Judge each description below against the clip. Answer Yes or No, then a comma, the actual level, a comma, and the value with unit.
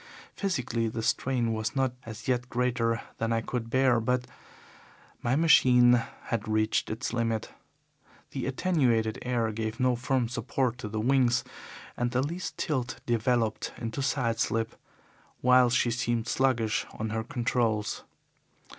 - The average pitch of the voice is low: Yes, low, 120 Hz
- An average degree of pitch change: No, narrow, 2.0 semitones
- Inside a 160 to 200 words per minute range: No, average, 140 wpm